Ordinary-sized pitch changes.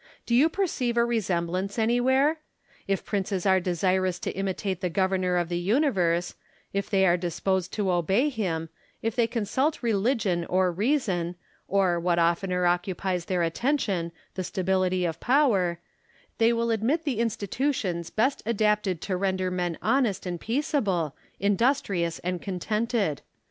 Yes: average, 4.6 semitones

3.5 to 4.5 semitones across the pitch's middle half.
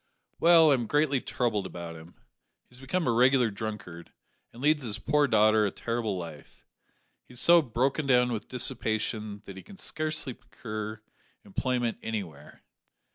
Yes: average, 4.2 semitones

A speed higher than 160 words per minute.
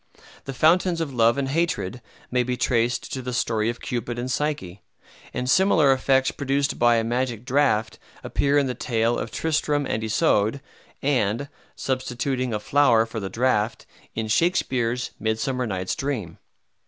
No: average, 155 wpm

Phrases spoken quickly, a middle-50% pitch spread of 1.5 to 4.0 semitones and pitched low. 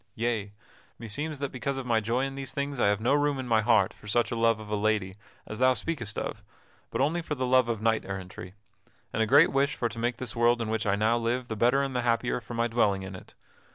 Yes: fast, 260 wpm; average, 3.1 semitones; low, 120 Hz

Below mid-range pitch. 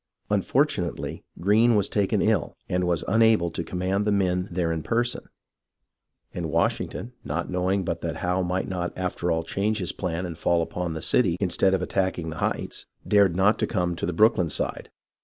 Yes: very low, 90 Hz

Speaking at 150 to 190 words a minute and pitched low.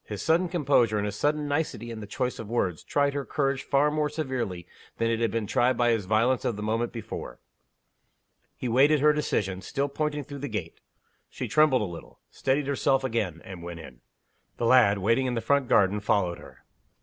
No: fast, 205 wpm; low, 120 Hz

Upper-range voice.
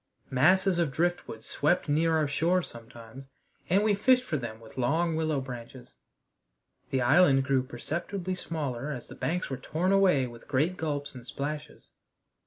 No: medium, 150 Hz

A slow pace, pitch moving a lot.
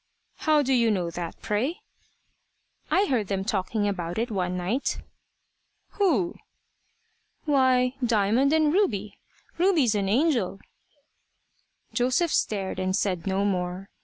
Yes: slow, 120 wpm; wide, 5.8 semitones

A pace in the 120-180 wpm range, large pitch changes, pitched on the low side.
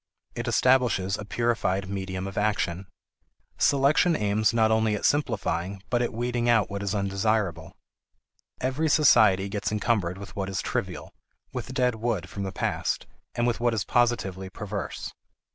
No: average, 155 wpm; average, 3.7 semitones; low, 105 Hz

